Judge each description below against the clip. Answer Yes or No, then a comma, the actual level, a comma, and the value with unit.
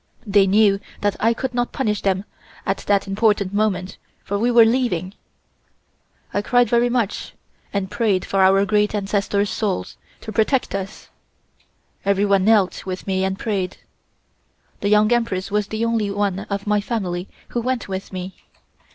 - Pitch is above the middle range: Yes, high, 205 Hz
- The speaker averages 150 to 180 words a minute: Yes, average, 160 wpm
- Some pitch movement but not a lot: No, narrow, 2.3 semitones